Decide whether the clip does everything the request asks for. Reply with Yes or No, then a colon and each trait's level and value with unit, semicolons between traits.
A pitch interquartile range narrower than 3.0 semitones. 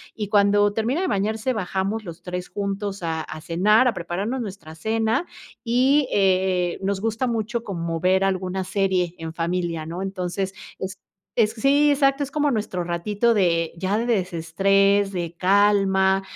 No: average, 3.4 semitones